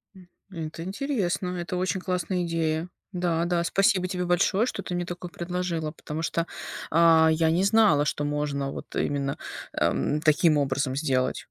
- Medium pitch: Yes, medium, 170 Hz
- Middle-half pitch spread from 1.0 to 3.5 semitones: Yes, average, 2.8 semitones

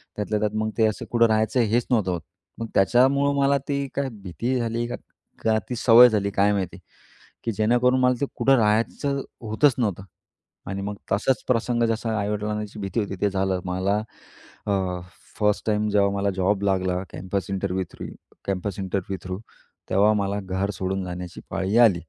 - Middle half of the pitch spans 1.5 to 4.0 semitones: Yes, average, 3.2 semitones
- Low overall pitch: Yes, low, 105 Hz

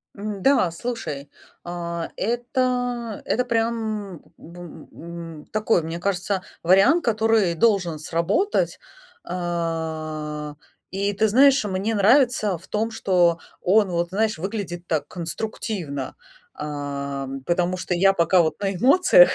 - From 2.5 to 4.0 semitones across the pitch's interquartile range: No, average, 4.7 semitones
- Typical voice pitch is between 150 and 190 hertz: Yes, medium, 185 Hz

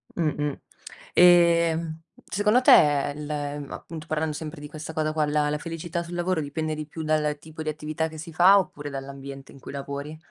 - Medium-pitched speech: Yes, medium, 155 Hz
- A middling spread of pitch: No, narrow, 2.0 semitones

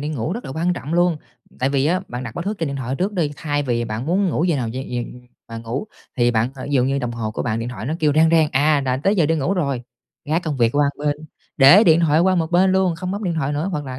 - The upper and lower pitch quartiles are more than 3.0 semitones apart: Yes, average, 5.0 semitones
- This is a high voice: No, medium, 145 Hz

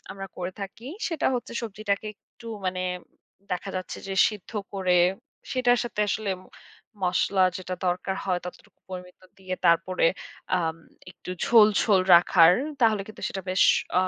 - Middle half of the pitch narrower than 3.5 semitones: Yes, average, 2.9 semitones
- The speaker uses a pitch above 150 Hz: Yes, high, 190 Hz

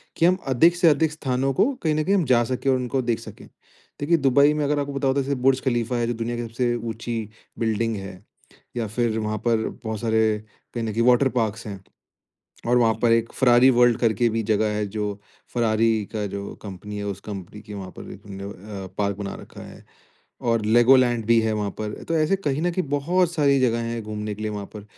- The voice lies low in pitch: Yes, low, 115 Hz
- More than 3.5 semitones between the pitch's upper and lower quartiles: Yes, average, 3.9 semitones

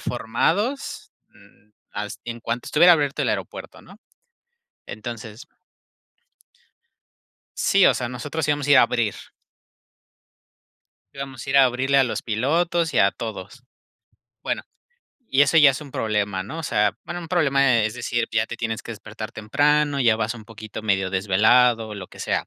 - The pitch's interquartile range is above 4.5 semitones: Yes, average, 4.9 semitones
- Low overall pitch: Yes, low, 120 Hz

